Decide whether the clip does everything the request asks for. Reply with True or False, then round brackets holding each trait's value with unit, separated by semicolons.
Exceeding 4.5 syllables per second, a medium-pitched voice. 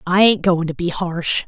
False (4.4 syllables/s; 175 Hz)